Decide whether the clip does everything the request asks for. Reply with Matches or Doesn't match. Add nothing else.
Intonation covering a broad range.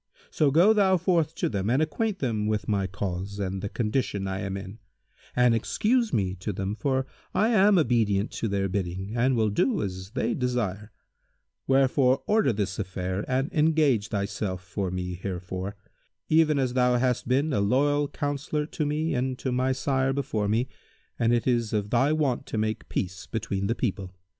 Matches